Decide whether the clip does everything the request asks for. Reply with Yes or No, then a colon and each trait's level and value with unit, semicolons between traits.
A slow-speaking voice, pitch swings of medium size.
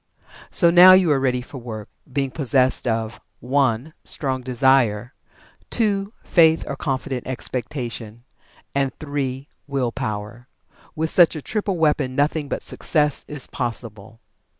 Yes: slow, 130 wpm; average, 3.7 semitones